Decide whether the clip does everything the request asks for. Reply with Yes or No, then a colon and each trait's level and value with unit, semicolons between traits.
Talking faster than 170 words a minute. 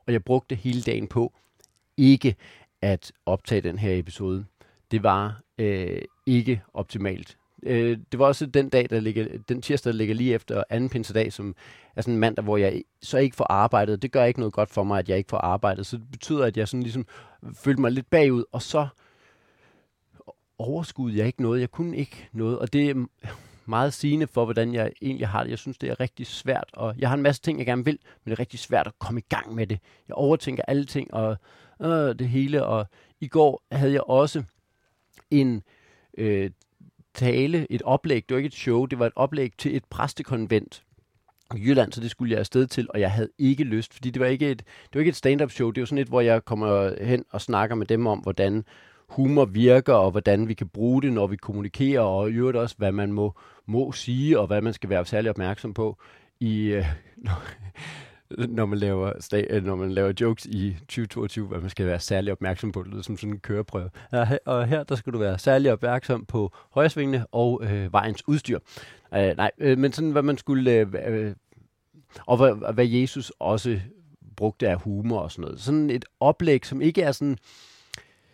Yes: average, 210 wpm